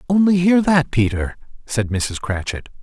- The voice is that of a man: Yes, male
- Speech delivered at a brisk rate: No, average, 150 wpm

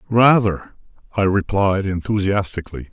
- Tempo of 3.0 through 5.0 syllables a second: Yes, 4.9 syllables/s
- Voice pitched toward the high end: No, low, 100 Hz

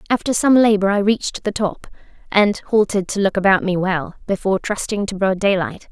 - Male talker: No, female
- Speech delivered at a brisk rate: No, average, 195 wpm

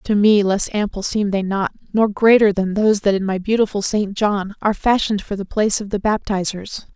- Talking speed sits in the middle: No, fast, 215 wpm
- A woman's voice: Yes, female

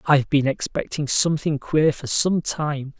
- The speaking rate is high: No, average, 160 wpm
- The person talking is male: Yes, male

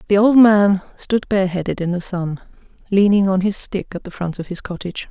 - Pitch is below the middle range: No, high, 190 Hz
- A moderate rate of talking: No, fast, 210 wpm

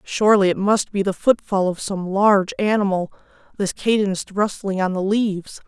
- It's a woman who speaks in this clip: Yes, female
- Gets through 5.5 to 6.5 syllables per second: No, 5.1 syllables/s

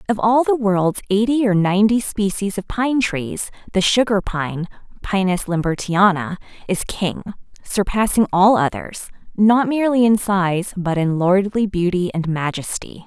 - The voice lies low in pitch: No, high, 200 Hz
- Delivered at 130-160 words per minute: Yes, average, 140 wpm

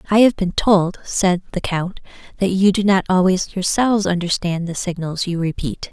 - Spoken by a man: No, female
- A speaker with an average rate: Yes, average, 180 wpm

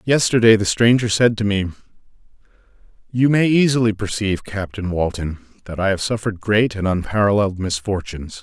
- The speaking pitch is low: Yes, low, 105 Hz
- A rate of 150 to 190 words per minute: No, average, 140 wpm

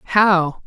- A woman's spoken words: Yes, female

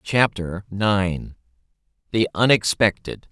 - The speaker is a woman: No, male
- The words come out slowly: Yes, slow, 55 wpm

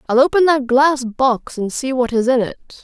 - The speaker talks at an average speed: No, fast, 235 wpm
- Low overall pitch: No, very high, 260 Hz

